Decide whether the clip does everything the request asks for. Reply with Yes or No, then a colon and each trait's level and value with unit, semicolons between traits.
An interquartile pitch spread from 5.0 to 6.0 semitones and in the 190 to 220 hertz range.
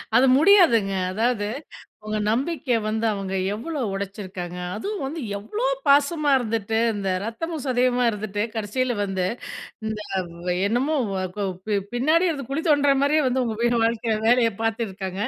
No: wide, 5.4 semitones; high, 230 Hz